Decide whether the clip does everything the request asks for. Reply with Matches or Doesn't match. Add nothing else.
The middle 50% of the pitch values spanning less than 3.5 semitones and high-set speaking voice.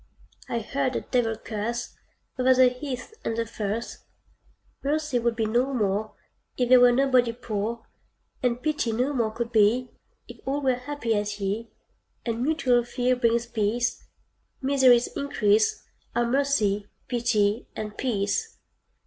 Matches